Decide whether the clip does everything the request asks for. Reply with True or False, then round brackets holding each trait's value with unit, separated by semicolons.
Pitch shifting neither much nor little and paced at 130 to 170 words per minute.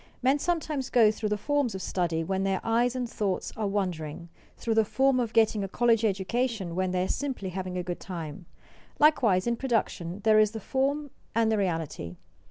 False (4.8 semitones; 195 wpm)